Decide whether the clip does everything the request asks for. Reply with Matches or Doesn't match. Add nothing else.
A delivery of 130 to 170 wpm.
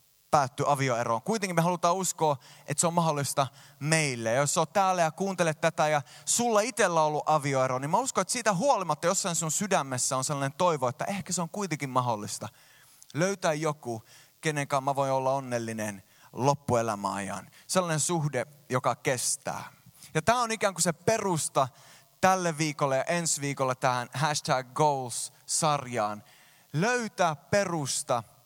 Matches